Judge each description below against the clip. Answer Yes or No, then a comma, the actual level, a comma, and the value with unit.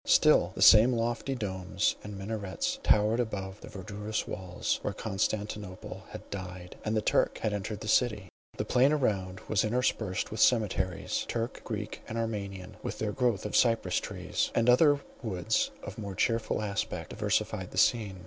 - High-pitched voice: No, low, 105 Hz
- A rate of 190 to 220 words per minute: No, average, 165 wpm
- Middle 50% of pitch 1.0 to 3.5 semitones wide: Yes, average, 2.9 semitones